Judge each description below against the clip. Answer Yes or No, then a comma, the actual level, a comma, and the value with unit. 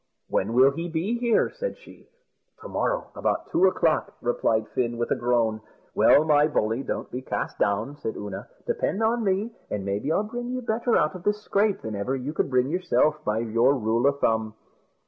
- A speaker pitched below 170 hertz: Yes, medium, 140 Hz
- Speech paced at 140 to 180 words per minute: No, average, 200 wpm